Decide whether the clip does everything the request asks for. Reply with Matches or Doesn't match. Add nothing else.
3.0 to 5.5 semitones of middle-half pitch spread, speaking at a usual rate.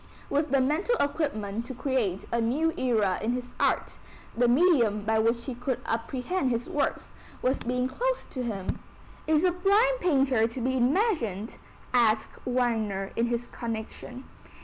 Matches